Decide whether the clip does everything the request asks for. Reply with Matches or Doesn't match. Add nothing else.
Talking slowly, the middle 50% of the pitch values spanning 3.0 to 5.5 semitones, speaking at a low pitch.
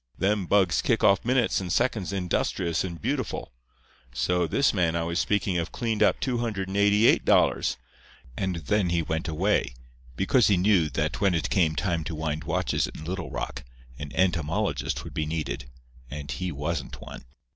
Doesn't match